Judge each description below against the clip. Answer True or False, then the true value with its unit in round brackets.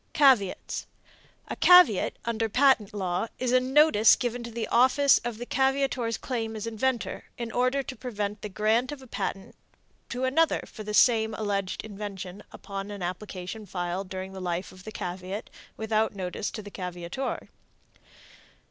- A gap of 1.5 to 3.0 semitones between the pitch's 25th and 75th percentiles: False (4.3 semitones)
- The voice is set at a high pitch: True (220 Hz)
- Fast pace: False (165 wpm)